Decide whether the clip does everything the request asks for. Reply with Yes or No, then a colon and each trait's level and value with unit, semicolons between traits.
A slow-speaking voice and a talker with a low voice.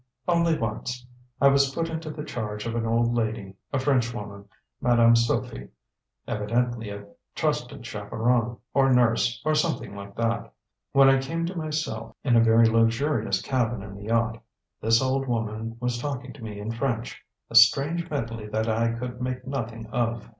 No: average, 170 wpm; low, 115 Hz